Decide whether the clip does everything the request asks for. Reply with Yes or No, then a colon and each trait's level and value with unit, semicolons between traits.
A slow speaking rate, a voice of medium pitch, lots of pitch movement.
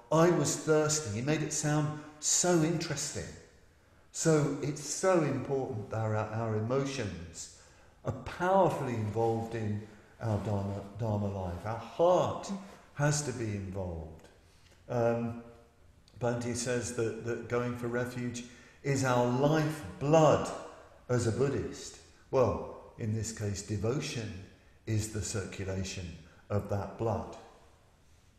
No: slow, 120 wpm; low, 115 Hz; wide, 5.7 semitones